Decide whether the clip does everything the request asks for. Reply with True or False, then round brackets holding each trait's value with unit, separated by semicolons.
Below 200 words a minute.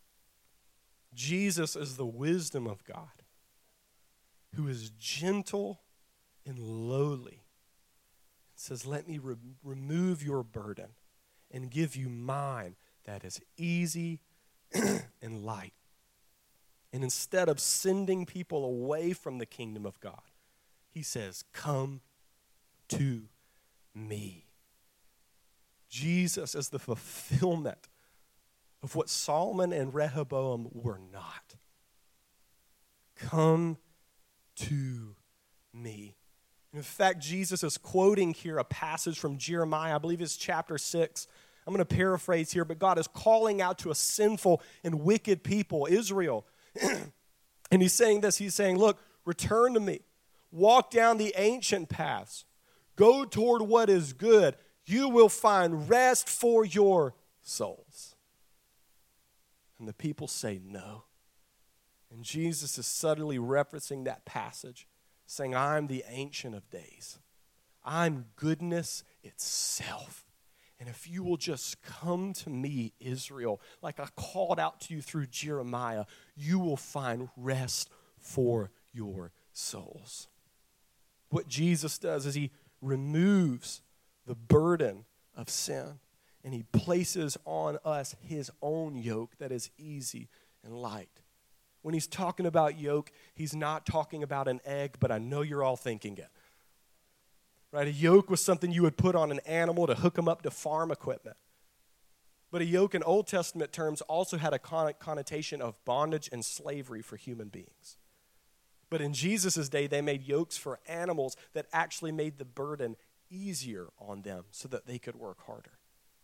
True (135 wpm)